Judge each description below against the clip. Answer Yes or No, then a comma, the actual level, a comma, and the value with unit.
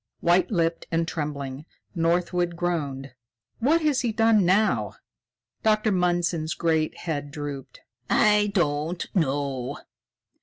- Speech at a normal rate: No, slow, 110 wpm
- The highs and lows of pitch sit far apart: No, average, 4.7 semitones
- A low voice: No, medium, 170 Hz